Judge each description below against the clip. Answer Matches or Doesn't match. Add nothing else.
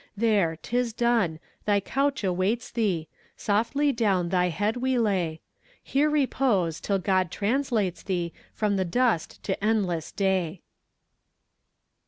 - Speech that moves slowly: Matches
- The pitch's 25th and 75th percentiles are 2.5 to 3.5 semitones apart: Doesn't match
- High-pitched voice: Matches